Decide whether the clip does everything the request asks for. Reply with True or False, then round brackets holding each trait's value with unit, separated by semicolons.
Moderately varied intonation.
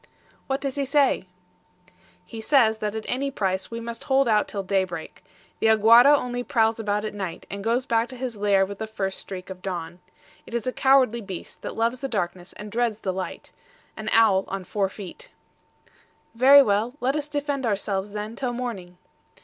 True (4.2 semitones)